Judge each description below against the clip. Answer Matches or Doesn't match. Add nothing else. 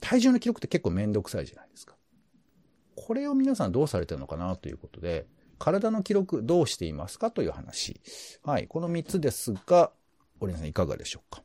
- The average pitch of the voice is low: Doesn't match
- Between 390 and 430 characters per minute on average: Matches